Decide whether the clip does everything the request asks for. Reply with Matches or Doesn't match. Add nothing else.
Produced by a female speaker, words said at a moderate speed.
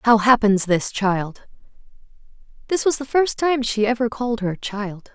Matches